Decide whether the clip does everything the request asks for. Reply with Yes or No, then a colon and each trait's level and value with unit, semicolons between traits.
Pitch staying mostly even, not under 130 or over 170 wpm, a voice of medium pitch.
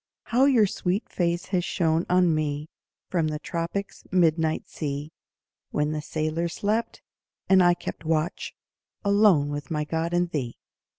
No: average, 3.0 semitones; average, 145 wpm; medium, 165 Hz